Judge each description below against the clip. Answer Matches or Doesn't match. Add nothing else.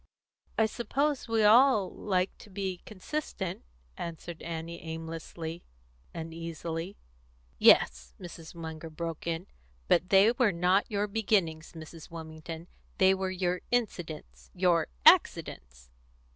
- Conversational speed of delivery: Doesn't match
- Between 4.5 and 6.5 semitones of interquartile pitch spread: Doesn't match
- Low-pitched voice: Doesn't match